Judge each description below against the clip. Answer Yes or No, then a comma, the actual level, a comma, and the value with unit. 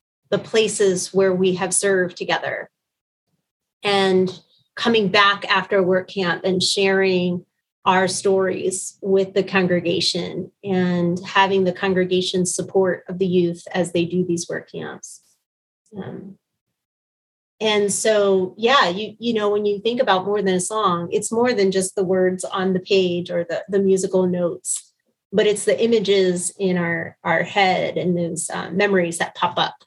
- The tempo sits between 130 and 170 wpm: Yes, average, 160 wpm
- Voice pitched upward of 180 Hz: Yes, high, 190 Hz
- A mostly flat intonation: Yes, narrow, 1.7 semitones